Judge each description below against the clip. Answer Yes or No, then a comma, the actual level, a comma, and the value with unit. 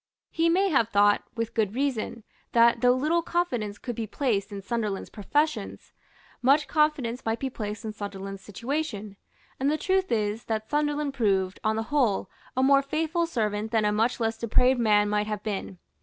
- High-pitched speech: Yes, high, 230 Hz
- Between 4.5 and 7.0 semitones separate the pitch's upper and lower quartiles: Yes, average, 5.2 semitones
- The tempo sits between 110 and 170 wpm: No, average, 180 wpm